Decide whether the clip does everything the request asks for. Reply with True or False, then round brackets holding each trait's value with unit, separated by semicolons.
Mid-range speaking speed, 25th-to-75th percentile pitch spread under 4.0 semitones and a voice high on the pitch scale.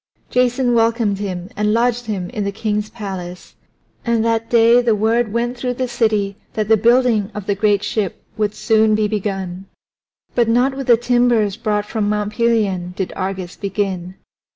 True (175 wpm; 2.8 semitones; 215 Hz)